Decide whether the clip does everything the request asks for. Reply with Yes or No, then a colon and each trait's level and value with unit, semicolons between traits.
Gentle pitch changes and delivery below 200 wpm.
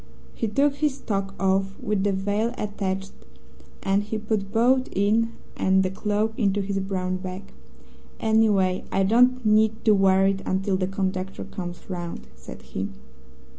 Yes: narrow, 2.3 semitones; average, 155 wpm